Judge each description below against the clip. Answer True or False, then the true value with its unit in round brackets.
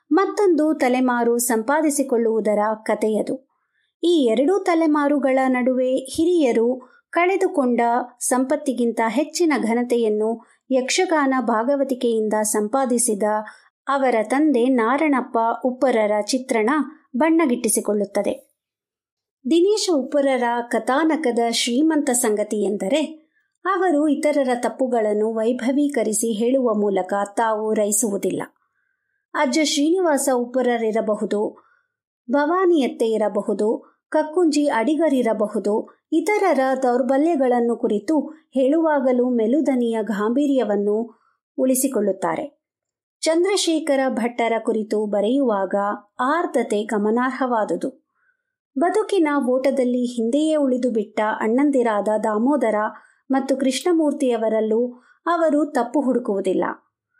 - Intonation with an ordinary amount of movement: True (4.9 semitones)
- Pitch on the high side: True (255 Hz)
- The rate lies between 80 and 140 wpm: False (70 wpm)